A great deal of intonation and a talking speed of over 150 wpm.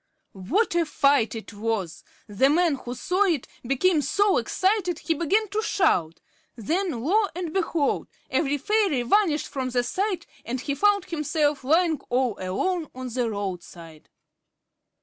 No: wide, 7.2 semitones; average, 145 wpm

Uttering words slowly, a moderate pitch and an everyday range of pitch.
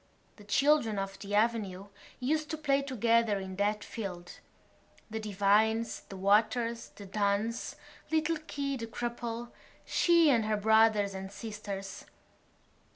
No: slow, 125 wpm; high, 220 Hz; average, 3.0 semitones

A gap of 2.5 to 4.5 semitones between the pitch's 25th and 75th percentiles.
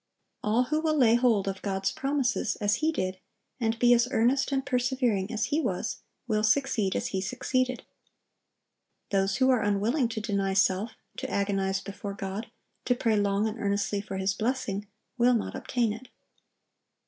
Yes: average, 4.0 semitones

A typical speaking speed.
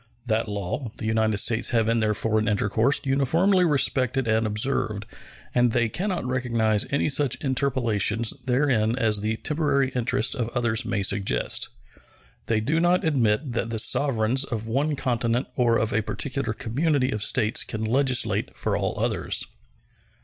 Yes: average, 155 wpm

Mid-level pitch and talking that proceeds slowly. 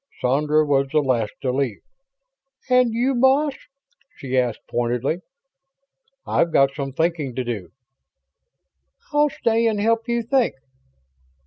Yes: medium, 150 Hz; slow, 125 wpm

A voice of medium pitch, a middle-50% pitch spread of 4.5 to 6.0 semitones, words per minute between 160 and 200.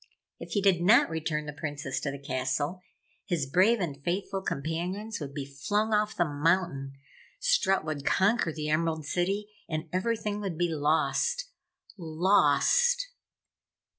No: medium, 170 Hz; wide, 5.6 semitones; average, 140 wpm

